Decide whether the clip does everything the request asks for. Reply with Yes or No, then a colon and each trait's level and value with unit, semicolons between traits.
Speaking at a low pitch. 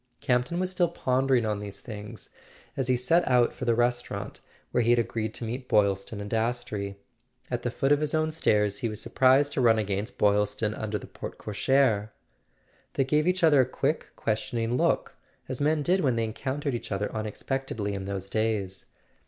Yes: low, 120 Hz